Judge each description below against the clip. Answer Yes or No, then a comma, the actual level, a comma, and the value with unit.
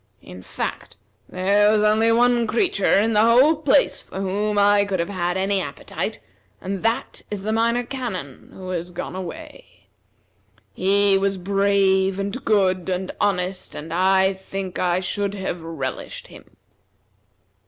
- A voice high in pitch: Yes, high, 195 Hz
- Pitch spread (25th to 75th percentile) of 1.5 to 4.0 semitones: Yes, narrow, 2.4 semitones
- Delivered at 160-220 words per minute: No, average, 150 wpm